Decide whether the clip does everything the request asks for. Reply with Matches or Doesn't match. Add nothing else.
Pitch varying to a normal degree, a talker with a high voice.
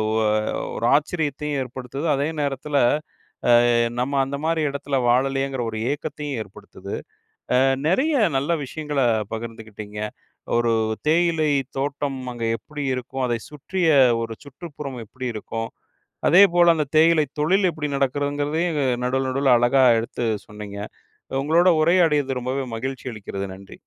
Doesn't match